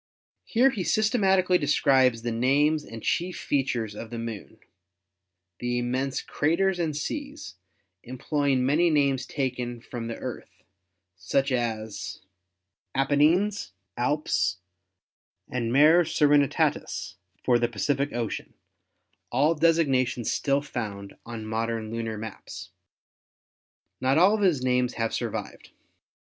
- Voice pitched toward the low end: Yes, low, 130 Hz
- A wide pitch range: No, average, 4.8 semitones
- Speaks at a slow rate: Yes, slow, 120 wpm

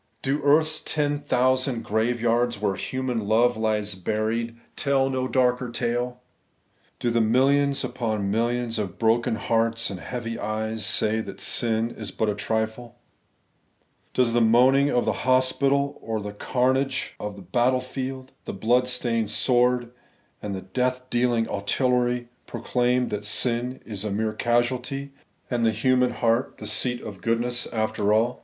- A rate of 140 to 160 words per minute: Yes, average, 150 wpm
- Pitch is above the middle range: No, low, 120 Hz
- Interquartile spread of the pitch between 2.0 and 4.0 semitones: Yes, narrow, 2.5 semitones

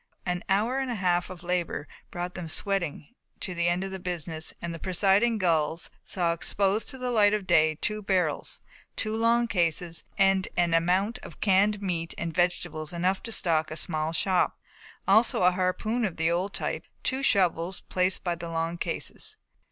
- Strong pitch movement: No, average, 3.1 semitones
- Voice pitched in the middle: Yes, medium, 180 Hz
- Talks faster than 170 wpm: Yes, average, 190 wpm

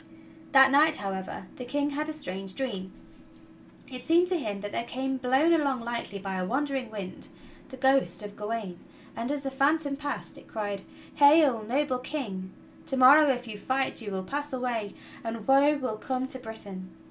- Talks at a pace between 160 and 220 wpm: Yes, average, 180 wpm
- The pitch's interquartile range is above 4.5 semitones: Yes, average, 5.2 semitones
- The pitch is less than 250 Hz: No, very high, 255 Hz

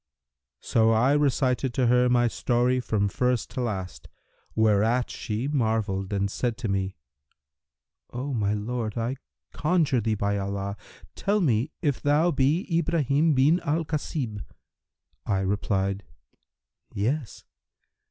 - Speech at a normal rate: No, slow, 125 wpm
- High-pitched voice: No, low, 120 Hz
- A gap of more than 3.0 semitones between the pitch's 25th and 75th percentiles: Yes, average, 5.2 semitones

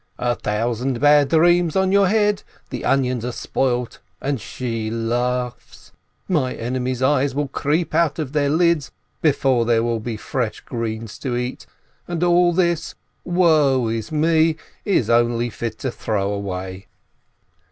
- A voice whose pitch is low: Yes, low, 130 Hz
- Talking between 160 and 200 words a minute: No, average, 145 wpm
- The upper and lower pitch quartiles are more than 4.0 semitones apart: Yes, average, 5.2 semitones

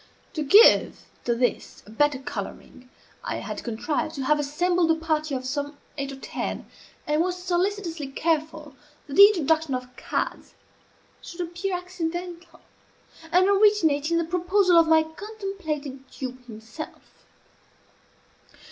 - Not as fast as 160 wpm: Yes, slow, 135 wpm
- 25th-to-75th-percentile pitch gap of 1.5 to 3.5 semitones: No, average, 4.3 semitones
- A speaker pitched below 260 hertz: No, very high, 320 Hz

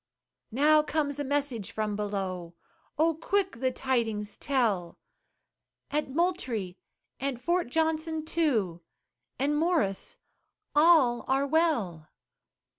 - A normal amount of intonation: No, wide, 7.0 semitones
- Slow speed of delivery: Yes, slow, 105 wpm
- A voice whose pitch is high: Yes, very high, 270 Hz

